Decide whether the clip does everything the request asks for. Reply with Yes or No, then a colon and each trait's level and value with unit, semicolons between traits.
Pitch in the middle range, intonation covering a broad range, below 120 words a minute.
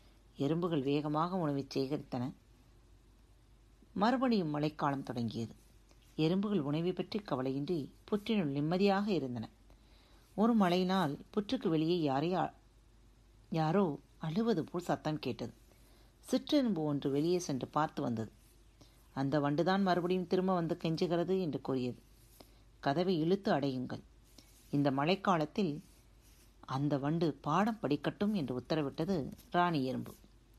Yes: medium, 150 Hz; wide, 6.4 semitones; average, 100 wpm